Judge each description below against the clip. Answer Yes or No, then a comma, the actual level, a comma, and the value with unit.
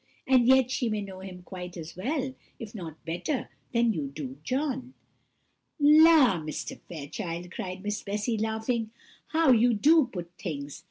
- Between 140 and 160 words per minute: Yes, average, 155 wpm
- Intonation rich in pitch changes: Yes, wide, 6.4 semitones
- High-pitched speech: Yes, high, 210 Hz